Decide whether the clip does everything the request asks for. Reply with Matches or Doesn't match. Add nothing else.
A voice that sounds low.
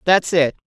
Doesn't match